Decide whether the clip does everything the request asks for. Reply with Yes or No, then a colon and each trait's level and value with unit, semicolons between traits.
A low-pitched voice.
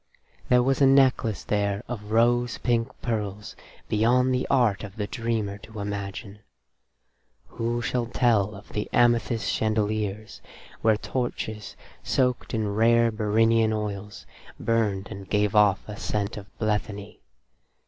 Yes: low, 110 Hz